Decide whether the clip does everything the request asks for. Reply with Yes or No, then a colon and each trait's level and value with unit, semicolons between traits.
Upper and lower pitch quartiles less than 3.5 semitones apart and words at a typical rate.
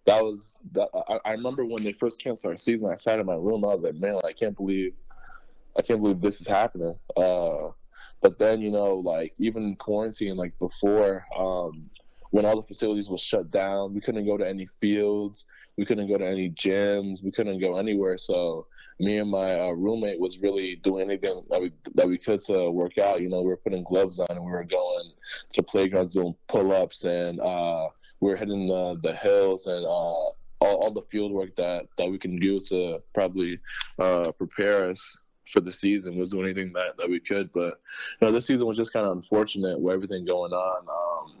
No: narrow, 2.5 semitones; fast, 215 wpm